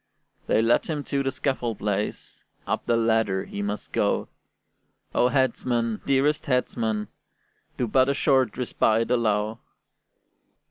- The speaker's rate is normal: No, slow, 130 wpm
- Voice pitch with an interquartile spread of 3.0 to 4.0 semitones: Yes, average, 3.4 semitones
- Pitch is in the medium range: No, low, 120 Hz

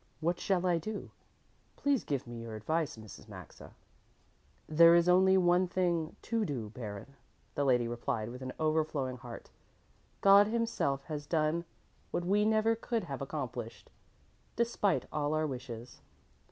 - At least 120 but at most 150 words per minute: Yes, average, 145 wpm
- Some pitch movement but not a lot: No, wide, 6.5 semitones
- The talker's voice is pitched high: No, medium, 155 Hz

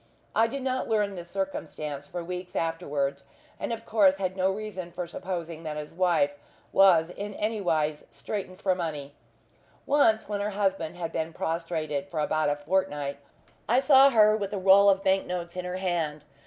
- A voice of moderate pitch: Yes, medium, 180 Hz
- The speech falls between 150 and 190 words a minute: Yes, average, 180 wpm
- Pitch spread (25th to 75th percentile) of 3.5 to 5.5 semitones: Yes, average, 3.9 semitones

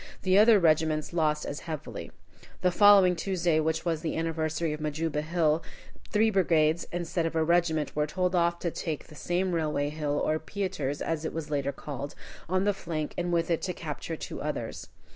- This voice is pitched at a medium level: Yes, medium, 165 Hz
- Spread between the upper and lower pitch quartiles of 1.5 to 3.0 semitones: Yes, narrow, 2.4 semitones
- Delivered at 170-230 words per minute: Yes, average, 190 wpm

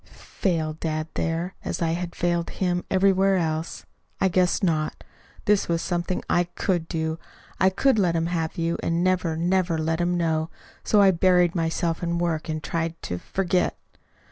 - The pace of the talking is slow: No, average, 170 wpm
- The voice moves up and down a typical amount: No, narrow, 2.0 semitones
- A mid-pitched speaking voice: Yes, medium, 170 Hz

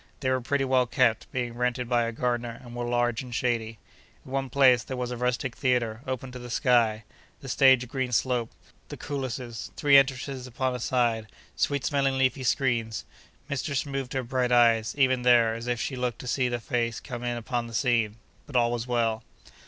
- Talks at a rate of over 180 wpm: Yes, fast, 205 wpm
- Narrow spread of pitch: Yes, narrow, 1.8 semitones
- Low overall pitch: Yes, low, 125 Hz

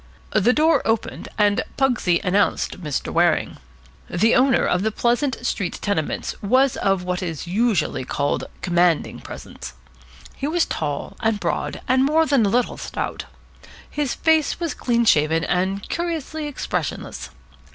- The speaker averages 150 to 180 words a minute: No, average, 140 wpm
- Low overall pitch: No, high, 225 Hz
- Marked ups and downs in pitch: Yes, wide, 7.1 semitones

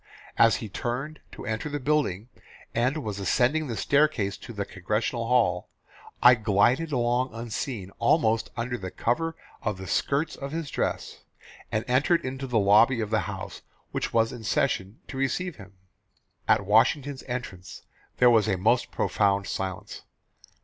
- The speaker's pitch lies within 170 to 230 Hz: No, low, 115 Hz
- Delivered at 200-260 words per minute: No, average, 155 wpm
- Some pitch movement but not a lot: Yes, average, 4.3 semitones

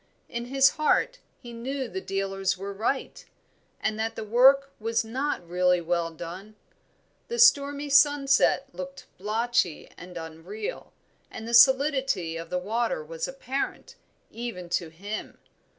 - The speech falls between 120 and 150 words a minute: Yes, slow, 135 wpm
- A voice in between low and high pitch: No, high, 225 Hz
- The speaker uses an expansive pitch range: Yes, wide, 6.9 semitones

